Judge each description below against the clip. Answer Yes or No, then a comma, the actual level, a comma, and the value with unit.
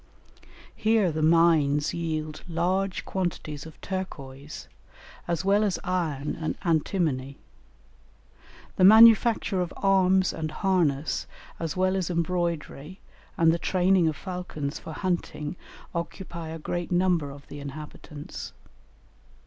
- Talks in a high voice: No, medium, 170 Hz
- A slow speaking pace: Yes, slow, 115 wpm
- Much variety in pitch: No, average, 3.4 semitones